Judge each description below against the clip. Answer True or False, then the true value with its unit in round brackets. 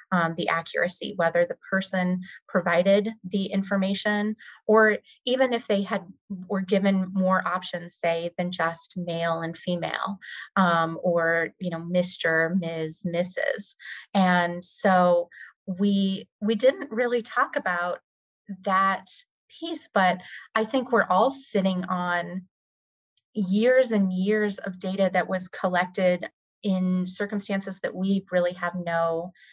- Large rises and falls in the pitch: False (2.4 semitones)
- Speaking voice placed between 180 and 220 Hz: True (185 Hz)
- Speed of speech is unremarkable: False (130 wpm)